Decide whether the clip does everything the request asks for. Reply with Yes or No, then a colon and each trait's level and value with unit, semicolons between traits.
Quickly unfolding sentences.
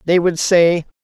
No: average, 175 wpm